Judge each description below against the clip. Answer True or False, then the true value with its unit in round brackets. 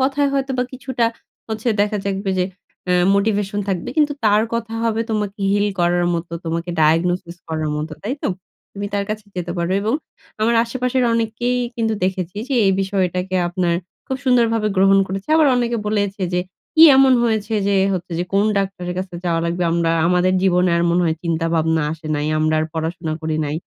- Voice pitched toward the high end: True (195 Hz)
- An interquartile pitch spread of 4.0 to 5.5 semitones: True (4.5 semitones)